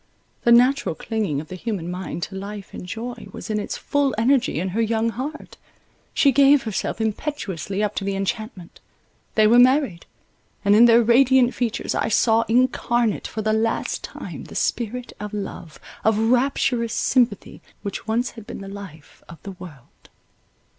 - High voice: Yes, high, 220 Hz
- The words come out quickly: No, average, 170 wpm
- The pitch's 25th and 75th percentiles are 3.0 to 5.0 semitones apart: Yes, average, 3.6 semitones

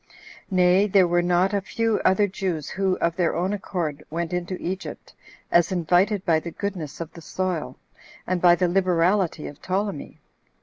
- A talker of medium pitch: Yes, medium, 180 Hz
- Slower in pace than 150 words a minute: No, average, 170 wpm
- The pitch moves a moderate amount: No, narrow, 2.2 semitones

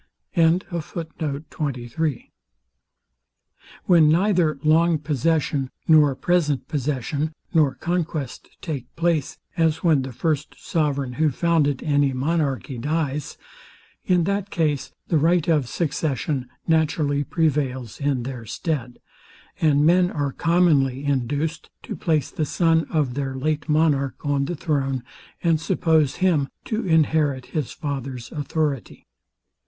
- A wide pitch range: No, average, 3.0 semitones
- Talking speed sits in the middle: No, slow, 115 wpm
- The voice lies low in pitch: No, medium, 150 Hz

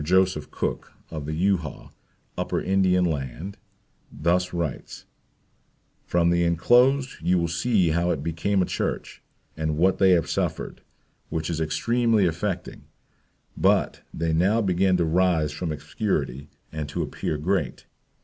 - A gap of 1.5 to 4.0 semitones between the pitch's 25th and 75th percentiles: Yes, average, 3.2 semitones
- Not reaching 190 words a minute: Yes, average, 140 wpm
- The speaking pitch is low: Yes, very low, 85 Hz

